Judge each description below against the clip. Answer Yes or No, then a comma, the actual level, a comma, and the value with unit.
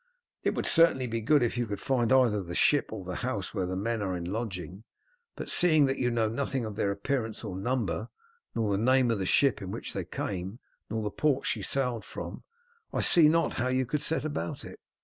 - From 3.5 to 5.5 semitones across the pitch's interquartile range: Yes, average, 4.8 semitones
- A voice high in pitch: No, low, 115 Hz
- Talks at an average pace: No, fast, 225 wpm